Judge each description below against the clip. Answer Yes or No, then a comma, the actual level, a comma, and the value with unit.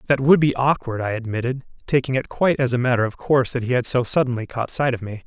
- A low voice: Yes, low, 125 Hz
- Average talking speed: No, fast, 260 wpm